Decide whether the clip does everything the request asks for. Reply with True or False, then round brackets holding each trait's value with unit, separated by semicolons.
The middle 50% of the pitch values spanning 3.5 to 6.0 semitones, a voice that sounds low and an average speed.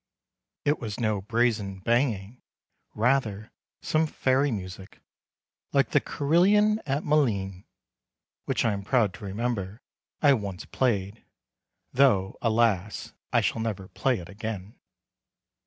False (4.9 semitones; 110 Hz; 120 wpm)